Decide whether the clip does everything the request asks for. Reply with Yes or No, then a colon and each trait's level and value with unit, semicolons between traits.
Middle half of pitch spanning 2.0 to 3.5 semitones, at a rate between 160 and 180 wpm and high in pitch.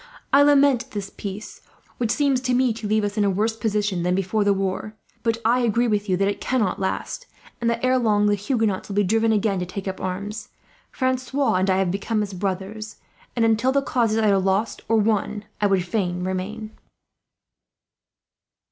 No: average, 3.0 semitones; average, 200 wpm; high, 210 Hz